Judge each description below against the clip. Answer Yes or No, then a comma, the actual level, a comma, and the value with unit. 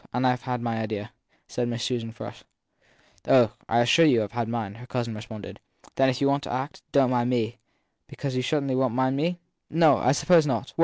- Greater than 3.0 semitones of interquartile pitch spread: No, narrow, 2.4 semitones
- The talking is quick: Yes, fast, 215 wpm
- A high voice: No, low, 125 Hz